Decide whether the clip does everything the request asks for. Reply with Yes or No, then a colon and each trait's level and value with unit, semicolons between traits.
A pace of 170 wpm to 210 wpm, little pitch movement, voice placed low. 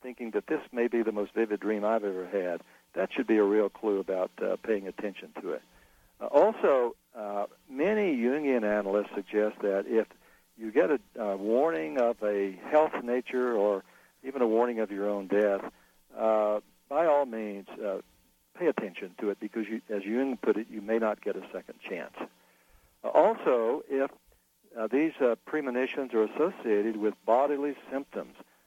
No: average, 175 wpm; average, 3.6 semitones; low, 110 Hz